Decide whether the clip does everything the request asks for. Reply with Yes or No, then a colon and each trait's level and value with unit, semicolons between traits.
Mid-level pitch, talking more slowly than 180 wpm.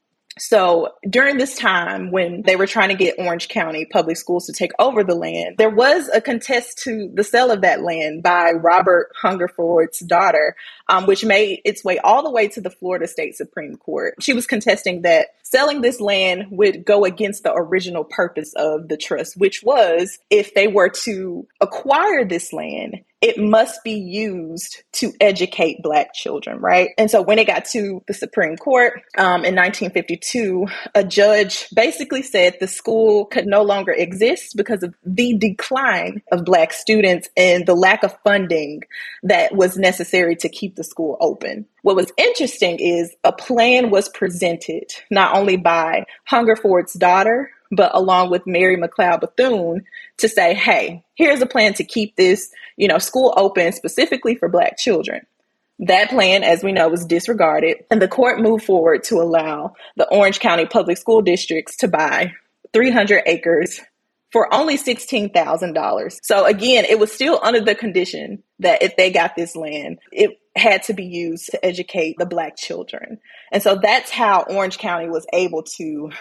No: high, 200 Hz; average, 170 wpm